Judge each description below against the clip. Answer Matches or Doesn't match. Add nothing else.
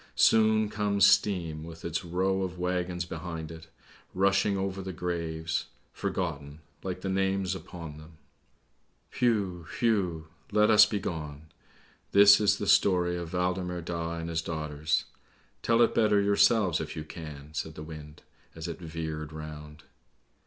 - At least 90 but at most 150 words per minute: Matches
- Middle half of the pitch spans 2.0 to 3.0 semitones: Doesn't match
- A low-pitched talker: Matches